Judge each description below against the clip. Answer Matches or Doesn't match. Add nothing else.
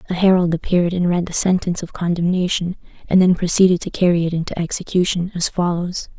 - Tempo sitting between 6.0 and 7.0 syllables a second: Matches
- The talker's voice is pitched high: Doesn't match